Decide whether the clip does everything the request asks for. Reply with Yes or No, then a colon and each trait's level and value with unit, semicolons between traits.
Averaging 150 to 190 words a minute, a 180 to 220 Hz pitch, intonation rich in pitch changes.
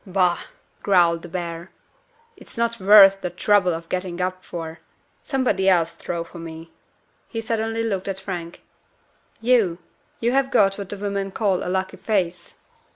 No: average, 160 wpm; high, 190 Hz; average, 3.1 semitones